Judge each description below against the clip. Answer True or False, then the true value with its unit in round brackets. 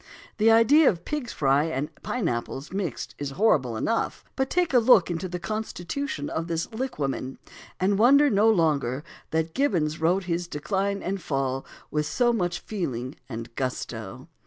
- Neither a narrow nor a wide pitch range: False (7.4 semitones)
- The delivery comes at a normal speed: True (160 wpm)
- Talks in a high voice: False (175 Hz)